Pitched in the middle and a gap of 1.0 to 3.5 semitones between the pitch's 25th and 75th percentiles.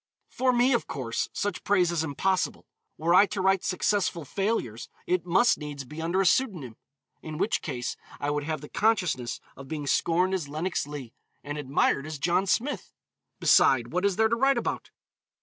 No: medium, 170 Hz; average, 5.3 semitones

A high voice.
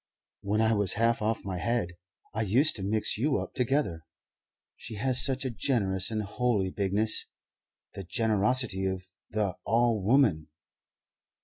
No: low, 110 Hz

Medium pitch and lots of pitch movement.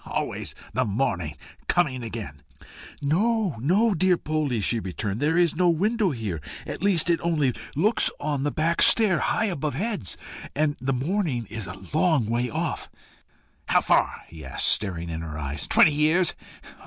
Yes: medium, 145 Hz; wide, 7.9 semitones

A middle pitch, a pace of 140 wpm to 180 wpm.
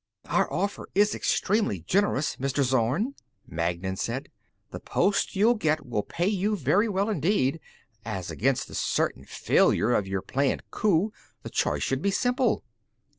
Yes: medium, 155 Hz; average, 150 wpm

